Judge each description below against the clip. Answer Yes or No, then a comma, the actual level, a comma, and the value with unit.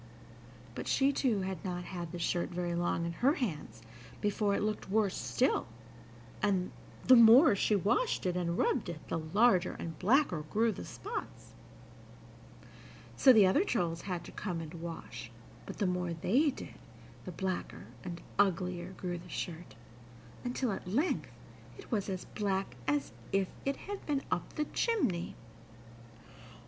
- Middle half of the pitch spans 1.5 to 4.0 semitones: No, average, 4.6 semitones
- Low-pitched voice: No, high, 190 Hz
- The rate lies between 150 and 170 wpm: Yes, average, 155 wpm